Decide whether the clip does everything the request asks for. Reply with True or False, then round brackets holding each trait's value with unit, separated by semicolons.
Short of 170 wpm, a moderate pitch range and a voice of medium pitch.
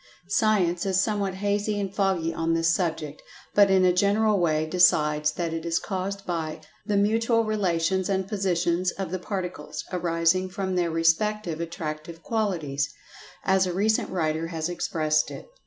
True (155 wpm; 3.2 semitones; 180 Hz)